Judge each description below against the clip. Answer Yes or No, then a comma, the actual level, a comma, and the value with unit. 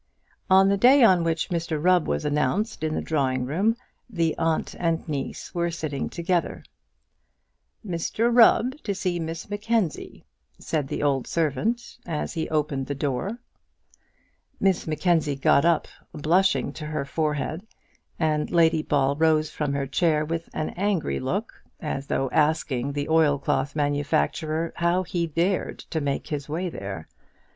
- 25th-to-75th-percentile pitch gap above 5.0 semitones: No, average, 3.3 semitones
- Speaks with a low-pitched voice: No, medium, 160 Hz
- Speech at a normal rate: Yes, average, 150 wpm